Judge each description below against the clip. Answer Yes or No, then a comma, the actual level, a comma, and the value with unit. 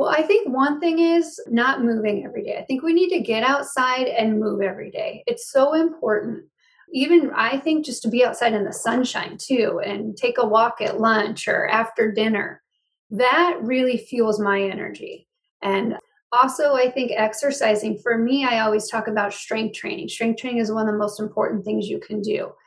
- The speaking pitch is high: Yes, high, 235 Hz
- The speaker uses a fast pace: No, average, 195 wpm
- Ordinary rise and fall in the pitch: Yes, average, 4.7 semitones